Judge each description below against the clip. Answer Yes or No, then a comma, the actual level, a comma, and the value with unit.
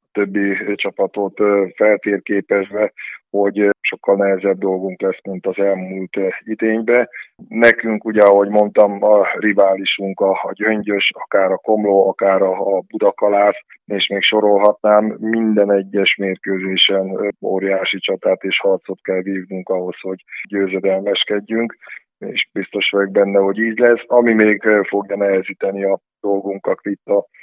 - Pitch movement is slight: Yes, narrow, 1.4 semitones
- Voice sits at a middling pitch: No, low, 100 Hz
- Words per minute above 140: No, average, 125 wpm